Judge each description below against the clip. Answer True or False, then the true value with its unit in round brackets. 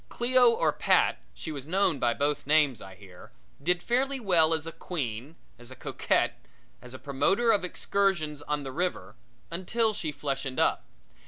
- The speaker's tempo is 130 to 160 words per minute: False (175 wpm)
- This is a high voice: False (155 Hz)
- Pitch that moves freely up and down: True (6.2 semitones)